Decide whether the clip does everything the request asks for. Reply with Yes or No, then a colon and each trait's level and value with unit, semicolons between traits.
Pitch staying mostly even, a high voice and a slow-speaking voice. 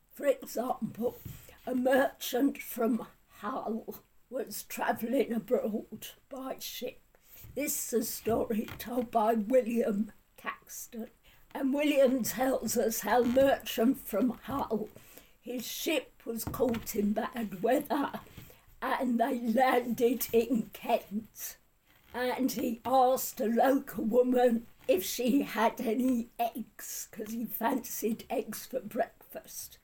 Yes: narrow, 2.2 semitones; high, 240 Hz; slow, 115 wpm